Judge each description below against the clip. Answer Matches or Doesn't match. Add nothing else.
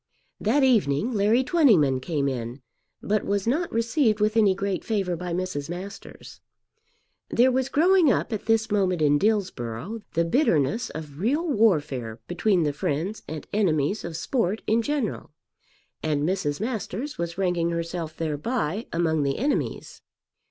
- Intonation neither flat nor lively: Doesn't match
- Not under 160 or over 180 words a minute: Doesn't match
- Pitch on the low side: Doesn't match